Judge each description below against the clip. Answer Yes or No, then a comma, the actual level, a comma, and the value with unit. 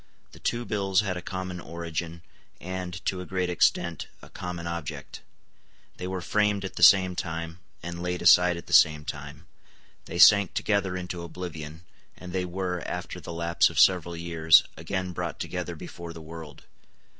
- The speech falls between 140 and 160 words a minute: No, average, 170 wpm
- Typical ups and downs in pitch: No, narrow, 1.8 semitones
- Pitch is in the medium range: No, very low, 90 Hz